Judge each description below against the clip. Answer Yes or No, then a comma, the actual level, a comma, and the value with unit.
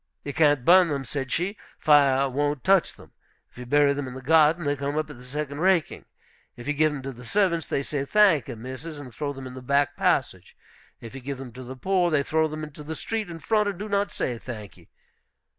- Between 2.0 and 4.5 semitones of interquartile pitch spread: Yes, average, 3.6 semitones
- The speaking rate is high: Yes, fast, 245 wpm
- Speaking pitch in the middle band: Yes, medium, 145 Hz